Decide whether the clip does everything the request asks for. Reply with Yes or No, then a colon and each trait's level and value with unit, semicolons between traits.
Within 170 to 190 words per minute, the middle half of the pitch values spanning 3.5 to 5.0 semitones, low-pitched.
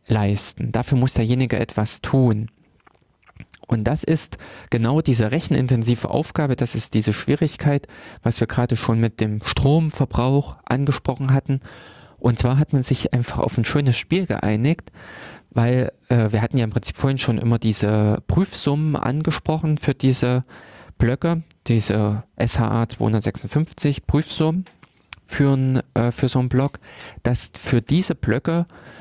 No: average, 140 wpm; average, 3.9 semitones; low, 125 Hz